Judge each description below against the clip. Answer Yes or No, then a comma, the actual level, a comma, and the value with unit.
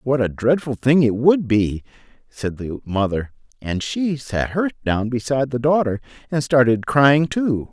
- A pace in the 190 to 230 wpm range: No, average, 170 wpm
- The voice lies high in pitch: No, low, 130 Hz